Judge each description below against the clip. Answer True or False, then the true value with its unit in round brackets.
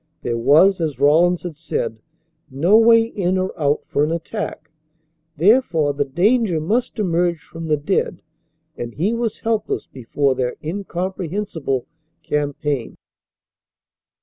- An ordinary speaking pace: False (125 wpm)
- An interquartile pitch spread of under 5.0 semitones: False (5.3 semitones)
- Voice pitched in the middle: True (165 Hz)